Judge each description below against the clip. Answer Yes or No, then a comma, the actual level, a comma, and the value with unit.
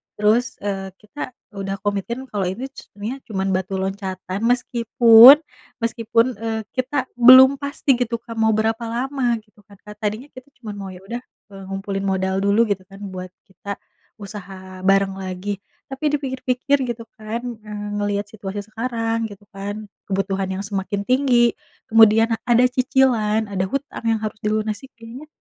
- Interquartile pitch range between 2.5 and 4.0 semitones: Yes, average, 3.5 semitones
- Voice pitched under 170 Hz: No, high, 215 Hz